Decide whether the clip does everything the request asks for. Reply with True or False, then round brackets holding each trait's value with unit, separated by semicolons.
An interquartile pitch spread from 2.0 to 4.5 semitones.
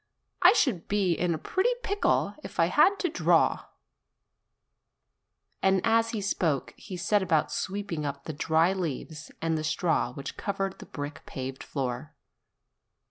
False (5.0 semitones)